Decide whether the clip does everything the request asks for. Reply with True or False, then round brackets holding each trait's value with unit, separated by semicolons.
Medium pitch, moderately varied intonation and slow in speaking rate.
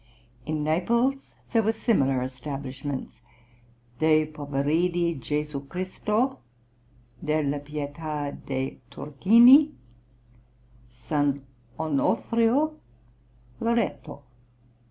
False (155 Hz; 7.5 semitones; 65 wpm)